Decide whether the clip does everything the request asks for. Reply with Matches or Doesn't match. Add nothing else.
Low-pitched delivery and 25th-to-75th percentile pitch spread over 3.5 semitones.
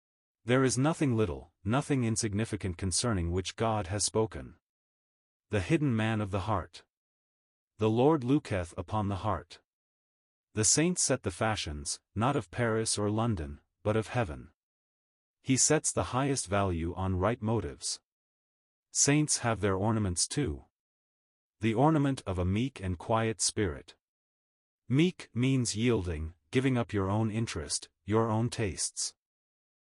Matches